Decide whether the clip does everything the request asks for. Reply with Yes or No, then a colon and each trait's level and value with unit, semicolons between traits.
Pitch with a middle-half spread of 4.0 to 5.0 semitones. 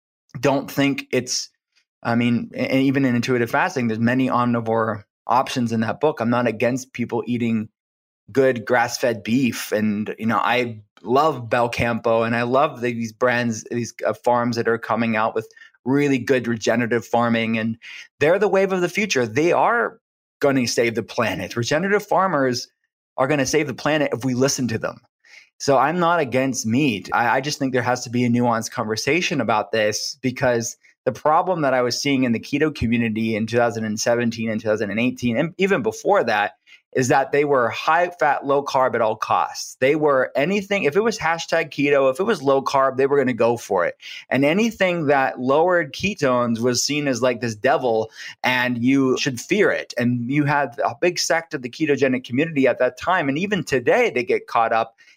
No: average, 3.4 semitones